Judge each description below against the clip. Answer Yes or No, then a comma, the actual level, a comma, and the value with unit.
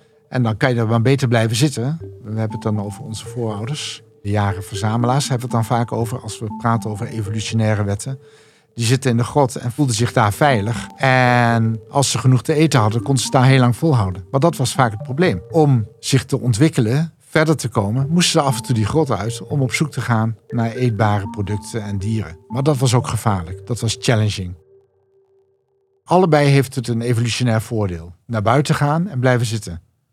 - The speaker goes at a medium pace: No, fast, 210 wpm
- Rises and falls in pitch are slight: No, average, 3.8 semitones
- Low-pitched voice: Yes, low, 120 Hz